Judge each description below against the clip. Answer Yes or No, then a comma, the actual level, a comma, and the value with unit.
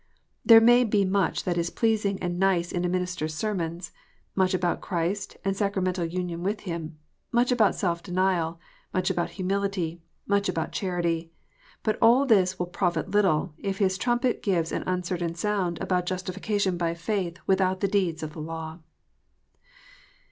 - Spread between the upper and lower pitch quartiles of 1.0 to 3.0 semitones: Yes, average, 2.7 semitones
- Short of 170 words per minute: Yes, average, 160 wpm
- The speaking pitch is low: No, medium, 185 Hz